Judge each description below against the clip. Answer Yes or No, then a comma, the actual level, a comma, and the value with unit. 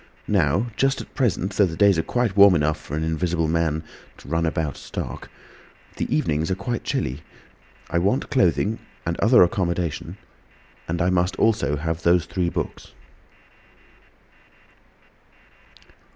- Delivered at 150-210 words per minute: No, slow, 135 wpm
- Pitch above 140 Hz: No, very low, 85 Hz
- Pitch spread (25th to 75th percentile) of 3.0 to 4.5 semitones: Yes, average, 3.6 semitones